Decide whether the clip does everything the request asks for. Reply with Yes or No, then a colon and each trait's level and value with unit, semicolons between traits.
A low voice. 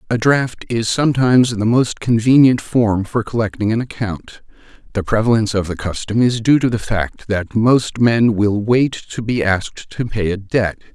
Yes: low, 110 Hz